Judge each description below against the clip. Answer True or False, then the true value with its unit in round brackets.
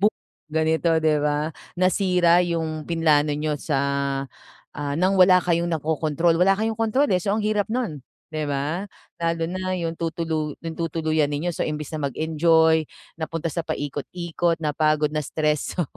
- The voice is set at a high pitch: False (160 Hz)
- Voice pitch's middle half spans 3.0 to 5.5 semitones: False (2.4 semitones)